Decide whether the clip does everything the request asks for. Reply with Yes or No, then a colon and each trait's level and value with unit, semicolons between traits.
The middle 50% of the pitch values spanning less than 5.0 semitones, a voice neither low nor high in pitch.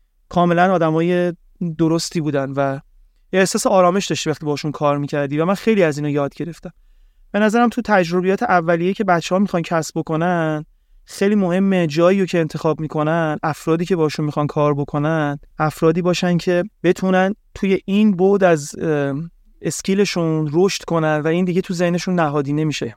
Yes: average, 3.2 semitones; medium, 170 Hz